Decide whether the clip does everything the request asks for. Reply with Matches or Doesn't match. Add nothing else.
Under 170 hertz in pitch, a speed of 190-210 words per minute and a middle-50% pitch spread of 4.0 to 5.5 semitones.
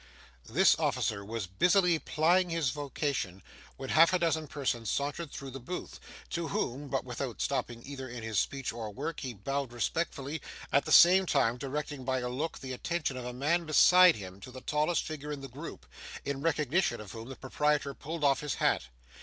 Matches